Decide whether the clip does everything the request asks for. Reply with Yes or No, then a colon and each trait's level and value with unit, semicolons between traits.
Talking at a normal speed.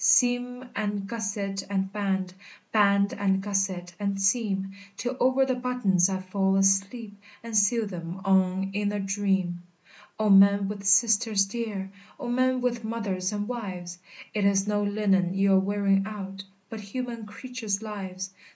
Yes: average, 150 wpm